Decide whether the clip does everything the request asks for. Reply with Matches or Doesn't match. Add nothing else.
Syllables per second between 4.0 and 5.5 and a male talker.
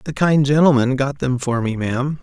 Matches